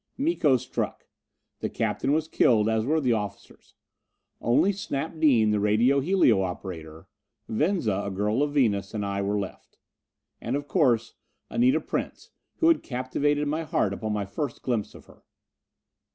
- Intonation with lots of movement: Yes, wide, 6.2 semitones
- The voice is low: Yes, low, 120 Hz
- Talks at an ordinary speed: Yes, average, 155 wpm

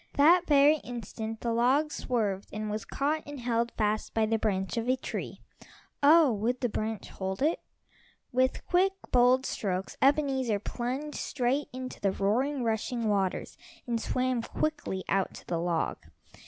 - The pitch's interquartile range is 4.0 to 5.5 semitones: Yes, average, 4.5 semitones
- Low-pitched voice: No, high, 240 Hz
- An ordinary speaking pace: Yes, average, 155 wpm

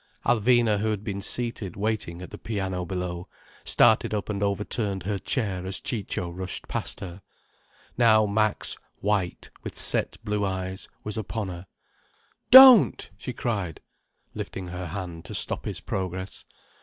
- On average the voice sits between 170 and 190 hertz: No, low, 100 Hz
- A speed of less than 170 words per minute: Yes, average, 145 wpm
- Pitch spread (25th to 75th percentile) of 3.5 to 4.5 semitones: No, average, 2.8 semitones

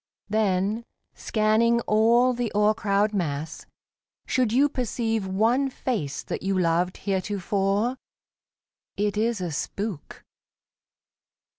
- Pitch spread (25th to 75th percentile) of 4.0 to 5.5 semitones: No, average, 3.4 semitones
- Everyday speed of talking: No, slow, 100 wpm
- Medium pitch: No, high, 210 Hz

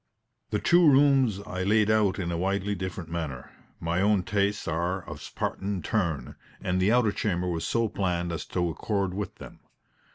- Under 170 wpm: No, average, 185 wpm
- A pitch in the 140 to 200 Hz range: No, very low, 95 Hz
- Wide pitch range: No, average, 3.2 semitones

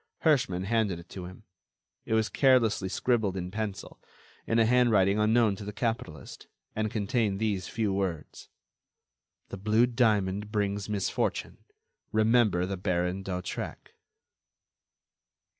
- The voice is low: Yes, low, 105 Hz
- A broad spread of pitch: No, average, 3.0 semitones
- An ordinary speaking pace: No, slow, 125 wpm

